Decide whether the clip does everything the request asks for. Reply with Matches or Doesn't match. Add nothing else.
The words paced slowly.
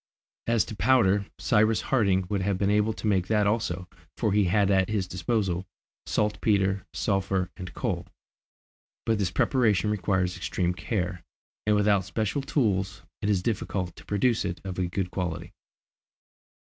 Doesn't match